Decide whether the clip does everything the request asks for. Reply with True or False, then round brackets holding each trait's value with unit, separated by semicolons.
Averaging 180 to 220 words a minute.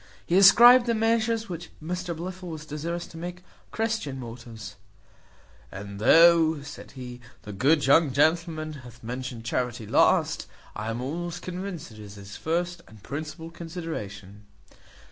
False (145 wpm)